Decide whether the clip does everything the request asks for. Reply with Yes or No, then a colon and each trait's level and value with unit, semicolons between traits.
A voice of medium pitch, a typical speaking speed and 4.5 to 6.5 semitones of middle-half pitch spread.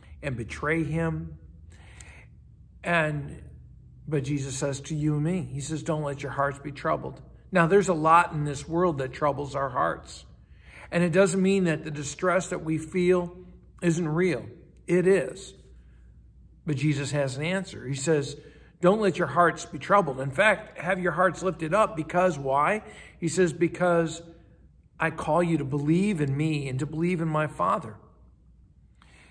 No: medium, 160 Hz; average, 170 wpm; average, 3.8 semitones